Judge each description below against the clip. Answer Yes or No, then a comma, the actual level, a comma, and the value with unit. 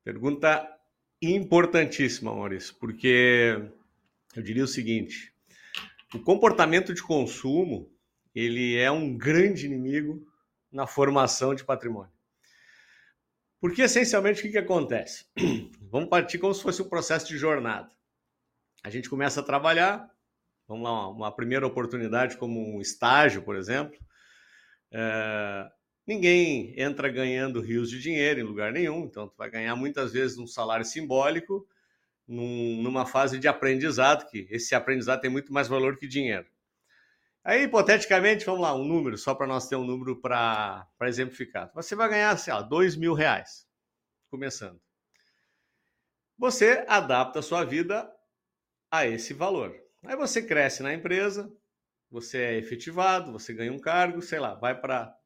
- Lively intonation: Yes, wide, 6.1 semitones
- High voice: No, low, 135 Hz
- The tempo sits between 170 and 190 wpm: No, average, 140 wpm